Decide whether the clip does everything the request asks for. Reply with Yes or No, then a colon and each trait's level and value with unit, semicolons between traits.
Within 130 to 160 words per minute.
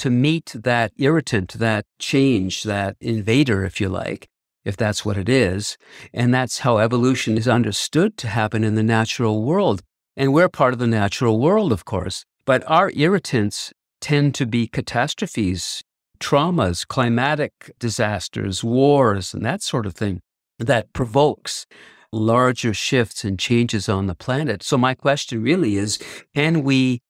Yes: average, 155 wpm